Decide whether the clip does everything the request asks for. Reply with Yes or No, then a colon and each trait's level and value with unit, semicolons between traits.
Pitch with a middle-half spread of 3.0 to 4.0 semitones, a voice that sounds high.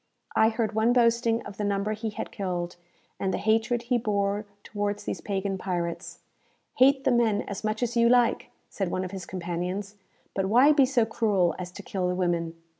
Yes: average, 3.6 semitones; high, 205 Hz